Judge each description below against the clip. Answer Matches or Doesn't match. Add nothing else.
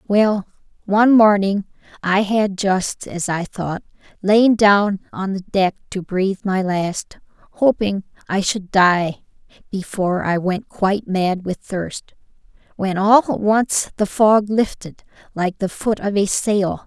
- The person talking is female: Matches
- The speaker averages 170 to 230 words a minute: Doesn't match